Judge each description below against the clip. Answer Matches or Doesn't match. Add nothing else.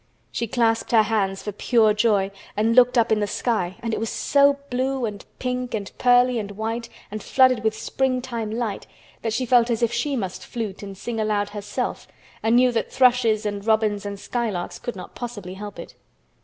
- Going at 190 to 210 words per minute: Matches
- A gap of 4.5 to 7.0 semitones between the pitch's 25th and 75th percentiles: Doesn't match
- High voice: Matches